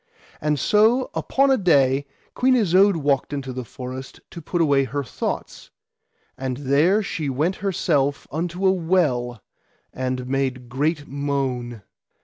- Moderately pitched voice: Yes, medium, 145 Hz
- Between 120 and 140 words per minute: Yes, slow, 135 wpm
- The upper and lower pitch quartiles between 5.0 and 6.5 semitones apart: Yes, average, 5.3 semitones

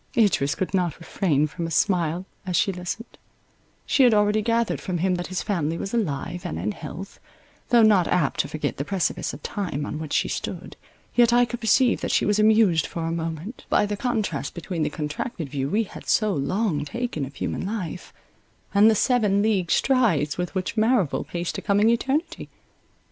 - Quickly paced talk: No, average, 195 wpm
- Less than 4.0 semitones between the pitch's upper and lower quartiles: No, average, 5.1 semitones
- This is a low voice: No, high, 190 Hz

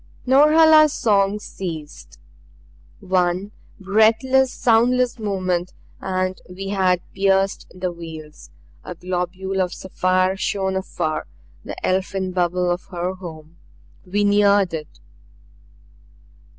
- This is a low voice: No, high, 190 Hz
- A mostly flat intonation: Yes, narrow, 2.3 semitones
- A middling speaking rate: No, slow, 100 wpm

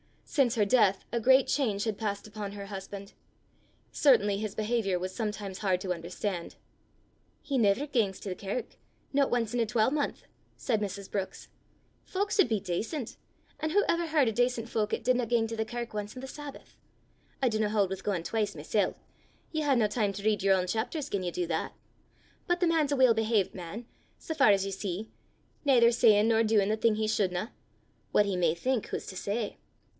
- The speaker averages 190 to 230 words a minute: Yes, average, 200 wpm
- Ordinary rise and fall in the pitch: Yes, average, 3.6 semitones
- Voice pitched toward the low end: No, high, 215 Hz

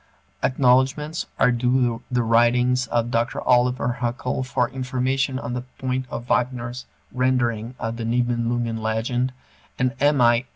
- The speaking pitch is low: Yes, low, 125 Hz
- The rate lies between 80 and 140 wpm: Yes, slow, 135 wpm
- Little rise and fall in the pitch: Yes, narrow, 1.4 semitones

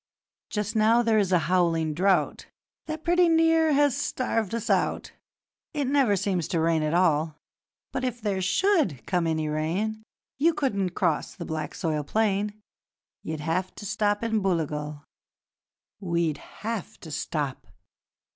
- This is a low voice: No, high, 190 Hz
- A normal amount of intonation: No, wide, 6.0 semitones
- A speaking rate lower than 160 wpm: Yes, average, 145 wpm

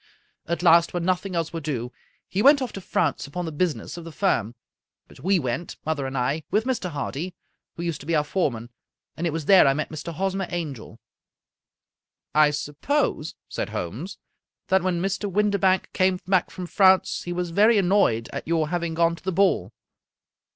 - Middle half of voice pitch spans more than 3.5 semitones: Yes, average, 4.0 semitones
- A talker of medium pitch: Yes, medium, 170 Hz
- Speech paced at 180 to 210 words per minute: Yes, average, 195 wpm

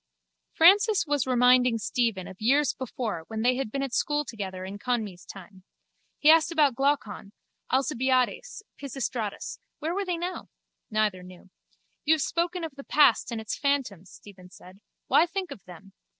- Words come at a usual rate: Yes, average, 165 wpm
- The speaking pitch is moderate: No, very high, 250 Hz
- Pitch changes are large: Yes, wide, 6.5 semitones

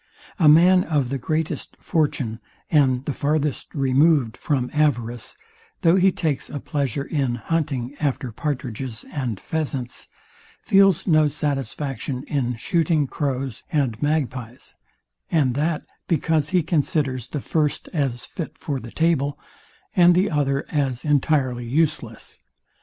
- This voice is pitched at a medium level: Yes, medium, 145 Hz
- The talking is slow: Yes, slow, 130 wpm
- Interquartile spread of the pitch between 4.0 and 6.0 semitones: No, average, 3.4 semitones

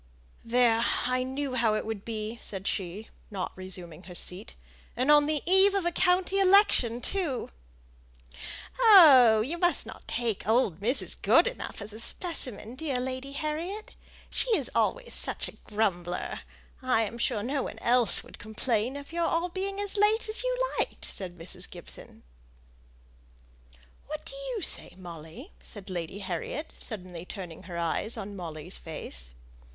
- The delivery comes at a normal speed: Yes, average, 155 wpm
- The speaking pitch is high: Yes, high, 240 Hz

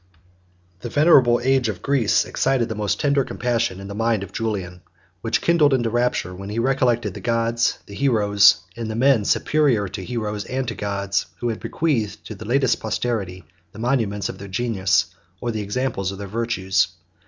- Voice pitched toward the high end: No, low, 115 Hz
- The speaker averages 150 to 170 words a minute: No, average, 185 wpm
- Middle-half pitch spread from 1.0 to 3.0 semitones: No, average, 3.6 semitones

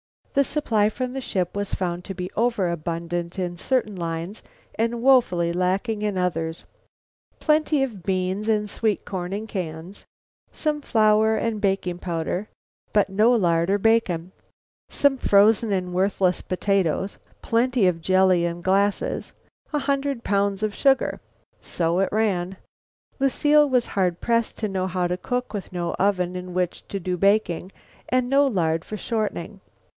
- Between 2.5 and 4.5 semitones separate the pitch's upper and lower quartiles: Yes, average, 4.1 semitones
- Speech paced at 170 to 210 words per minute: No, average, 155 wpm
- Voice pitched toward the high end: Yes, high, 195 Hz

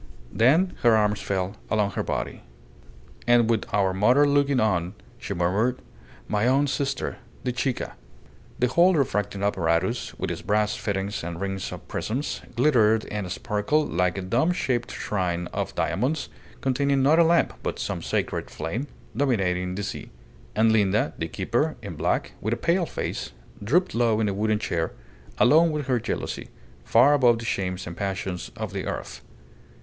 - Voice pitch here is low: Yes, low, 110 Hz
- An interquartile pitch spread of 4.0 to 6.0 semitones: Yes, wide, 5.5 semitones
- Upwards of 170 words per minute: No, average, 165 wpm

